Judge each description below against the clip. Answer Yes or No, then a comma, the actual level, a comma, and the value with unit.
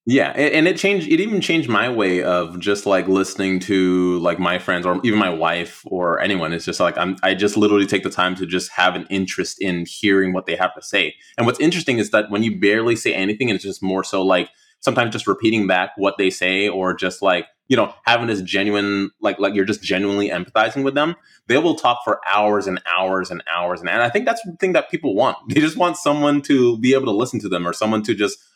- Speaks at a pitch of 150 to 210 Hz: No, low, 100 Hz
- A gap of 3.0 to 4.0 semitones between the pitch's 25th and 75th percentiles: Yes, average, 3.4 semitones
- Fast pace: Yes, fast, 245 wpm